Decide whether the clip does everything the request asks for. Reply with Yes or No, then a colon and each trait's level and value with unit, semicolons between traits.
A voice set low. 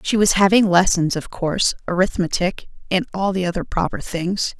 No: medium, 185 Hz